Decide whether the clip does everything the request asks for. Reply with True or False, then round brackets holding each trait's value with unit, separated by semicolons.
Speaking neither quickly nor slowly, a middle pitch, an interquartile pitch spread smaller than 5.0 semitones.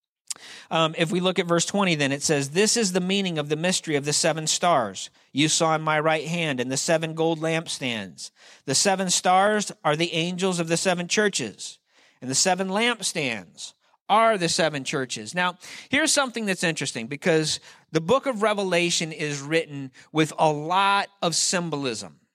True (180 wpm; 165 Hz; 3.7 semitones)